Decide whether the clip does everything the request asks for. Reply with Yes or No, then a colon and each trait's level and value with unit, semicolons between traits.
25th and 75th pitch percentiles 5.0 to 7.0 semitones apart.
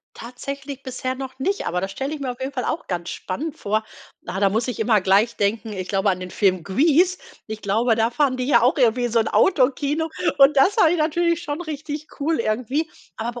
Yes: average, 5.3 semitones